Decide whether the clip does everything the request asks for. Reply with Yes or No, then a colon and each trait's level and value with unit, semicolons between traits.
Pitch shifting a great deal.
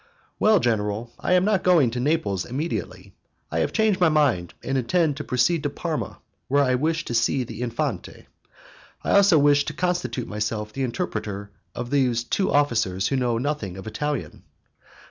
Yes: wide, 5.8 semitones